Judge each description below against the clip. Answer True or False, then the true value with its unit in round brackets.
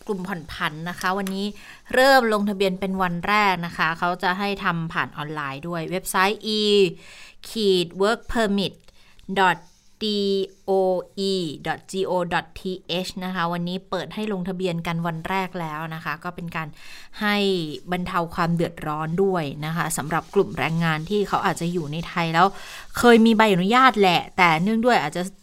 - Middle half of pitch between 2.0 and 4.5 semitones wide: True (2.6 semitones)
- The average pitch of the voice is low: False (185 Hz)